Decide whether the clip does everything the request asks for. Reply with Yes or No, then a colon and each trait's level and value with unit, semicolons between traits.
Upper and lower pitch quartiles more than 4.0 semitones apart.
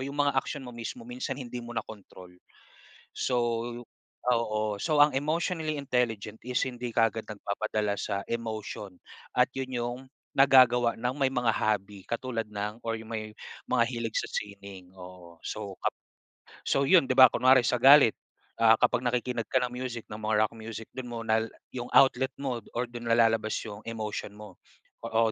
No: average, 3.1 semitones